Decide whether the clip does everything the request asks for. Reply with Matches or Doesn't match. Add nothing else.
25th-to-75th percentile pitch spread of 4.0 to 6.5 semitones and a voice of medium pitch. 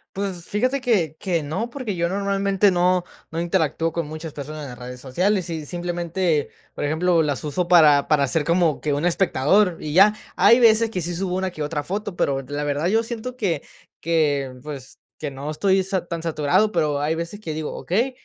Matches